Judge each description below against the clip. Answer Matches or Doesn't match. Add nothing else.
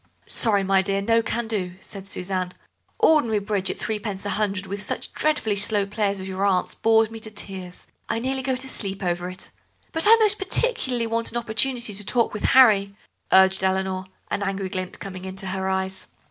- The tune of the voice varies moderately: Matches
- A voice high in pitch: Matches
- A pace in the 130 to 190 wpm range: Doesn't match